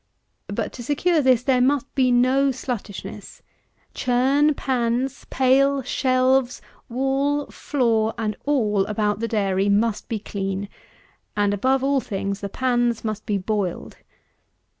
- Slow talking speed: Yes, slow, 130 wpm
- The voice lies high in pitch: Yes, high, 245 Hz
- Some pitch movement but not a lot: Yes, average, 4.2 semitones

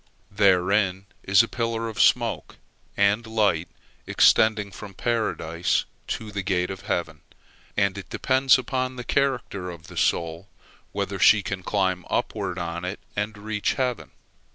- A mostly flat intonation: No, average, 3.6 semitones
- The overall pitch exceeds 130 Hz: No, low, 100 Hz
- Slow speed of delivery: No, average, 145 wpm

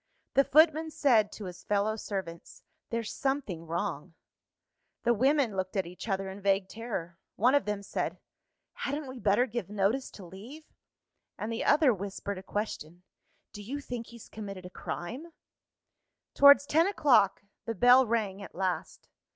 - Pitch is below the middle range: No, high, 215 Hz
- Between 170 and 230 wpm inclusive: No, average, 160 wpm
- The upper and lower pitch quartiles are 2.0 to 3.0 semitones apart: No, average, 5.1 semitones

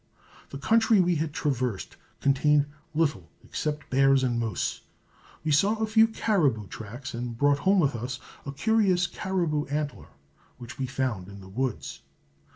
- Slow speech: No, average, 155 wpm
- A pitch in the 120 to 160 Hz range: Yes, medium, 140 Hz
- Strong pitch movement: Yes, wide, 6.1 semitones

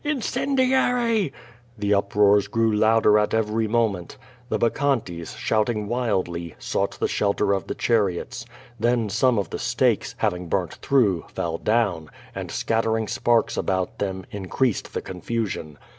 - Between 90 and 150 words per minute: Yes, average, 145 wpm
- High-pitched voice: No, low, 105 Hz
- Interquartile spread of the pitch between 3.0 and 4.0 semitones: Yes, average, 3.7 semitones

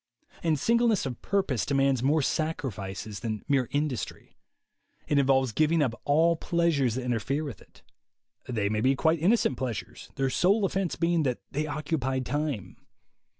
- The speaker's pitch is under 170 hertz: Yes, medium, 140 Hz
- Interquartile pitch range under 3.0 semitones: No, average, 4.3 semitones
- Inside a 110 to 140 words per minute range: No, average, 155 wpm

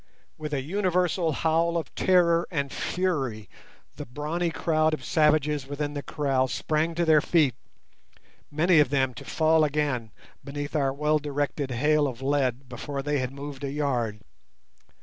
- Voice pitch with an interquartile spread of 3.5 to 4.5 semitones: No, average, 2.7 semitones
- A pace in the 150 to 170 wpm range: Yes, average, 155 wpm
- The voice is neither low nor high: Yes, medium, 145 Hz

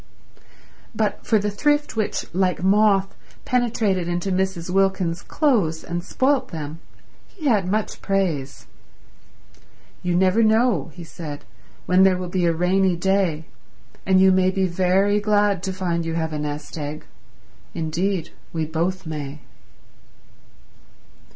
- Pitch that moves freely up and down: No, average, 3.2 semitones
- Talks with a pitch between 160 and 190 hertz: Yes, medium, 185 Hz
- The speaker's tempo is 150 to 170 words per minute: No, slow, 135 wpm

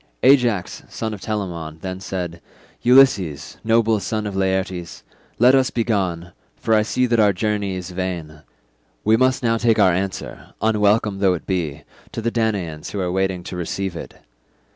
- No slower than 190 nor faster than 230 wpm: No, average, 170 wpm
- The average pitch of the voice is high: No, low, 100 Hz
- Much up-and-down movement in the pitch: No, average, 3.8 semitones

